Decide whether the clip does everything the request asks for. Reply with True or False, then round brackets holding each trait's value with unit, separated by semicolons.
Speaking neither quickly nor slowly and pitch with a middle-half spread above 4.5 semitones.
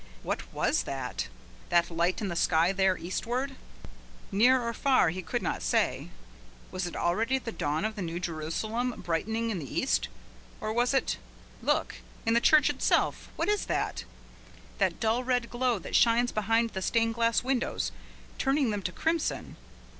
True (170 wpm; 5.4 semitones)